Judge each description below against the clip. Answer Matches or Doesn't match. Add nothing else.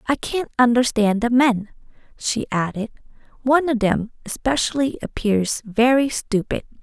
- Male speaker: Doesn't match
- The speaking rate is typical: Doesn't match